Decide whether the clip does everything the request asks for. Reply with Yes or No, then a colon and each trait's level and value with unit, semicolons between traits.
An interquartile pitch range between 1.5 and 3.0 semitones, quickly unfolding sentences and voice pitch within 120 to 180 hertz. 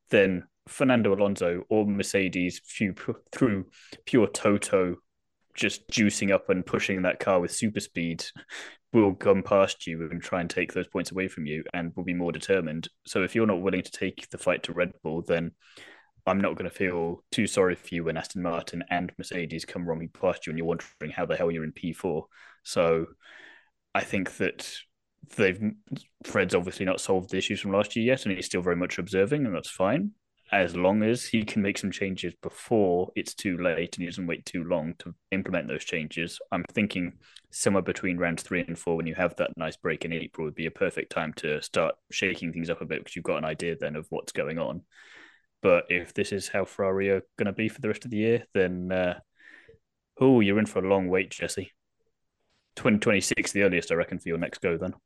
No: average, 2.7 semitones; fast, 215 wpm; very low, 90 Hz